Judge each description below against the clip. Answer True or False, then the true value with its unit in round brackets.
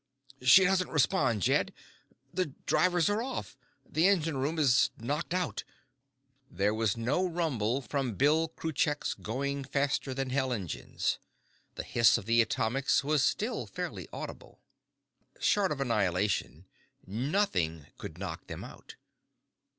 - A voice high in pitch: False (140 Hz)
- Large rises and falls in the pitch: True (6.1 semitones)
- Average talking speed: False (130 wpm)